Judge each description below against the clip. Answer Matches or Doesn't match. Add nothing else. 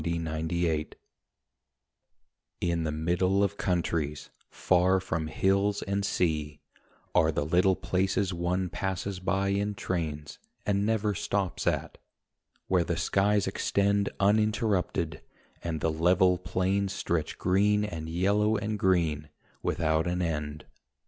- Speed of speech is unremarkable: Doesn't match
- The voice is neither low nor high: Doesn't match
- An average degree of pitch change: Matches